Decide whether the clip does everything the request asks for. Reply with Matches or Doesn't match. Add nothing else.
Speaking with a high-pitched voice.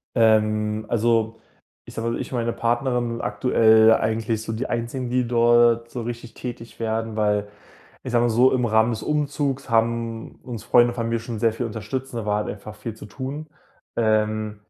Doesn't match